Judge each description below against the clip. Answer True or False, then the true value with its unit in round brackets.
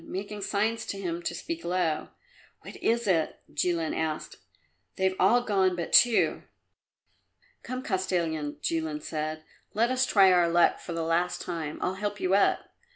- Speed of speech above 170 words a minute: False (155 wpm)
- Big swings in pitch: False (3.7 semitones)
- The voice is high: False (180 Hz)